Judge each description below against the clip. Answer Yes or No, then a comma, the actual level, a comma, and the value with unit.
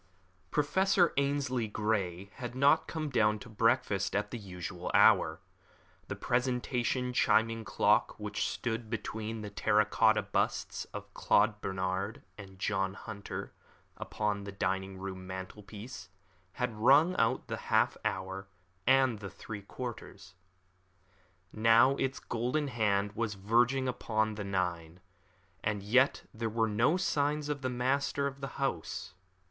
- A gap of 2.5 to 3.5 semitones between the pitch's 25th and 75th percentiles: No, average, 4.3 semitones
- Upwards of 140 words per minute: No, slow, 135 wpm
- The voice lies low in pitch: Yes, low, 110 Hz